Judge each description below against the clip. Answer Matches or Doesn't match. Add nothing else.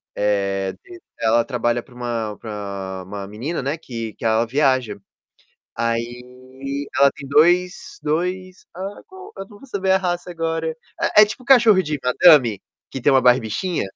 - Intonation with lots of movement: Matches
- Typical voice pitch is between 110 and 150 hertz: Matches